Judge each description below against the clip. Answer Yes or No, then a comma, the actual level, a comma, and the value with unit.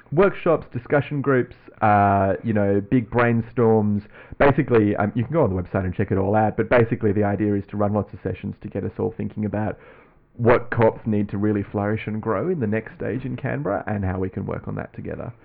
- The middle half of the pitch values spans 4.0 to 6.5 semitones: No, narrow, 2.6 semitones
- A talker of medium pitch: No, low, 110 Hz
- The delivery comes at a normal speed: No, fast, 230 wpm